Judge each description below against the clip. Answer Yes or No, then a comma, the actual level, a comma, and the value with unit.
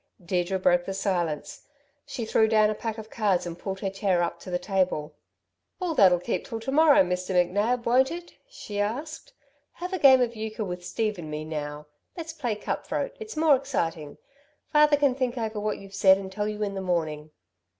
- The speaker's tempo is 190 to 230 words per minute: Yes, fast, 205 wpm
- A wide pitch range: Yes, wide, 5.7 semitones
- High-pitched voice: Yes, high, 205 Hz